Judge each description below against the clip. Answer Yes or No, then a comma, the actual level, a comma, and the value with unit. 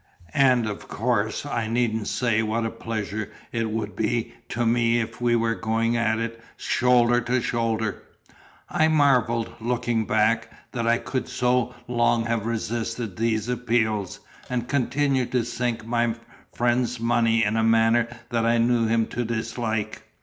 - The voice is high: No, low, 115 Hz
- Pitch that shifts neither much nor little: No, narrow, 1.3 semitones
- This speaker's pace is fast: No, average, 155 wpm